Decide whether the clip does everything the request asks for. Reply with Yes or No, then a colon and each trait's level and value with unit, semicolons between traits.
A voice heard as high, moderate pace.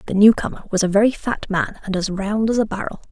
No: high, 205 Hz; fast, 270 wpm